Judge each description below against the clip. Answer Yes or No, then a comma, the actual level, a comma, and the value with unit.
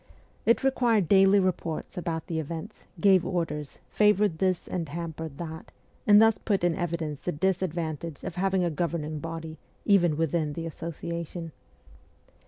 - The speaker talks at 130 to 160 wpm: Yes, average, 150 wpm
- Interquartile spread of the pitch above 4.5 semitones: No, average, 2.9 semitones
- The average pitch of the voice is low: No, medium, 170 Hz